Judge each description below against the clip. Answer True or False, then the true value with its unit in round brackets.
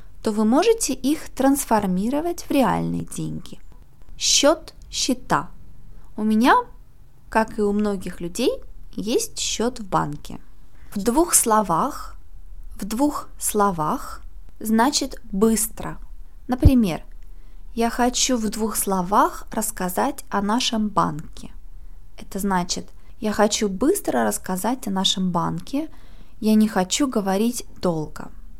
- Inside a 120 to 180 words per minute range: False (110 wpm)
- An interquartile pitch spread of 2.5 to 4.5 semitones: False (5.1 semitones)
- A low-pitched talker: False (220 Hz)